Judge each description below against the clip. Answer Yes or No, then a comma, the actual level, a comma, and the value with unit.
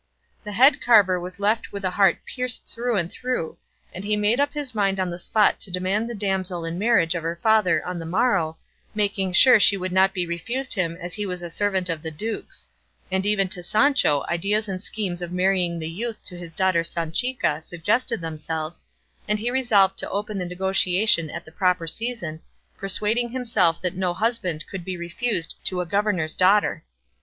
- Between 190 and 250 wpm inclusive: Yes, average, 195 wpm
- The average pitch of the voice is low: No, high, 190 Hz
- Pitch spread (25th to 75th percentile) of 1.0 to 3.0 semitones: No, average, 3.7 semitones